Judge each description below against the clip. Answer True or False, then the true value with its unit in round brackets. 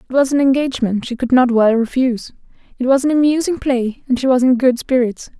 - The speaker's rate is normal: False (225 wpm)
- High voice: True (255 Hz)